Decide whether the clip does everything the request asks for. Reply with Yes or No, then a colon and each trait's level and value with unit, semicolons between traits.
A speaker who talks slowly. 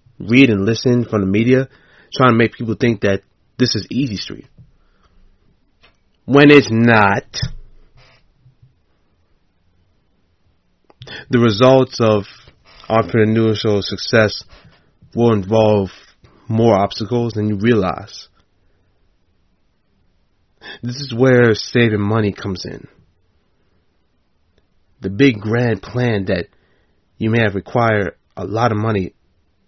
Yes: slow, 105 wpm